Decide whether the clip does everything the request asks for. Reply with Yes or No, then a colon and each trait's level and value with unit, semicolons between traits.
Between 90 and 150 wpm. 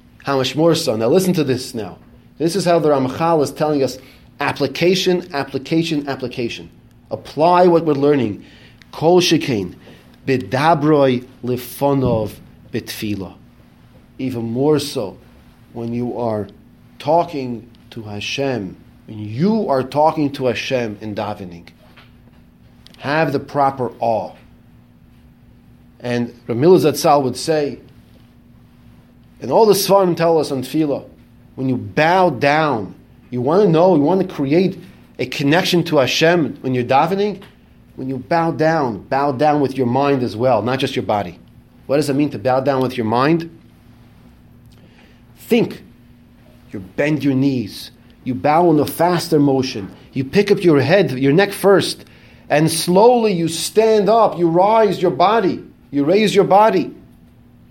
Yes: average, 145 wpm